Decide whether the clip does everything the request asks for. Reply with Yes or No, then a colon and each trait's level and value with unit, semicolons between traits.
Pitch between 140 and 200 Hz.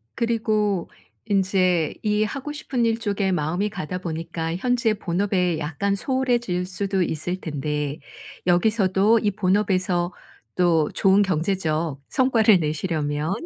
Yes: high, 190 Hz